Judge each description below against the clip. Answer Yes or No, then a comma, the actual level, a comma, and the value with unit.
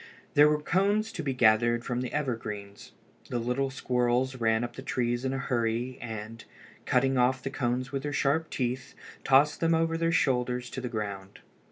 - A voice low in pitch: Yes, low, 125 Hz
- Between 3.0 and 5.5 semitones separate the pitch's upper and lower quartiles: No, narrow, 2.6 semitones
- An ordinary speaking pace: Yes, average, 185 wpm